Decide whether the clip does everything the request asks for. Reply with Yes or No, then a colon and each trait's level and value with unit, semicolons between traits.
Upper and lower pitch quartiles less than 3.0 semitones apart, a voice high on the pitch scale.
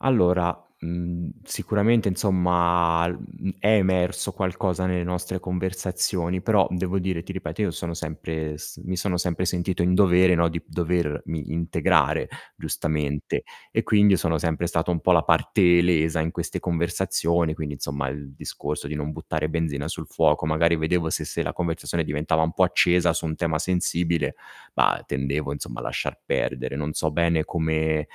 No: narrow, 2.4 semitones; very low, 85 Hz